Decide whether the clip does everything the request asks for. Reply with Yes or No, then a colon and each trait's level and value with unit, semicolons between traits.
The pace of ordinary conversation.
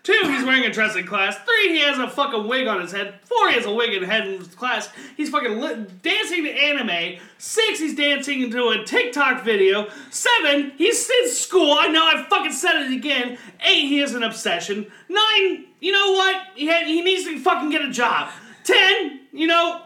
No: fast, 215 wpm